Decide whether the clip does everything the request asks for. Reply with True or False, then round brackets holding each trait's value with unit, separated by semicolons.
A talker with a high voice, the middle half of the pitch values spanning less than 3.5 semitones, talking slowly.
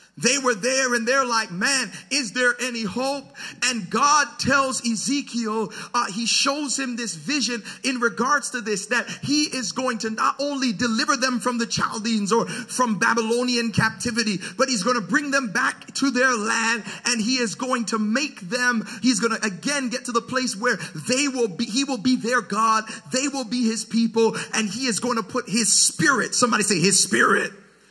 False (240 Hz; 2.5 semitones; 200 wpm)